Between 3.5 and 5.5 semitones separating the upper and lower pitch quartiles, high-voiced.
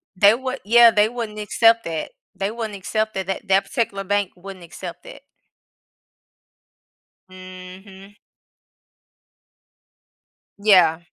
No: average, 2.7 semitones; high, 200 Hz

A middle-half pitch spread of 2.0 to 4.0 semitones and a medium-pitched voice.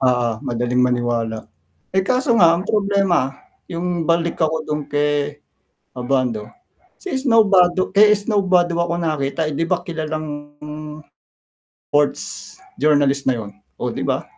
No: average, 5.1 semitones; medium, 155 Hz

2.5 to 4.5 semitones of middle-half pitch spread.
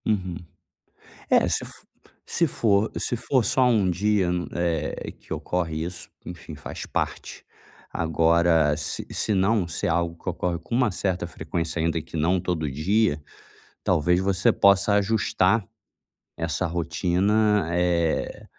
Yes: average, 3.4 semitones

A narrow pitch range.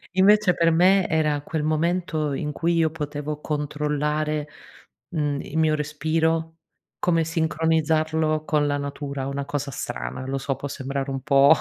Yes: narrow, 2.0 semitones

